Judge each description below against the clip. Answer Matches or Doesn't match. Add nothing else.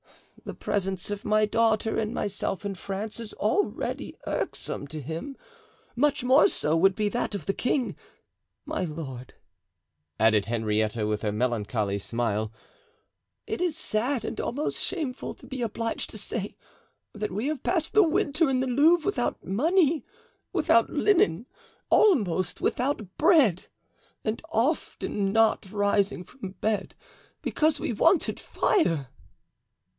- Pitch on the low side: Doesn't match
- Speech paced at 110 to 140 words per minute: Matches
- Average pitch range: Doesn't match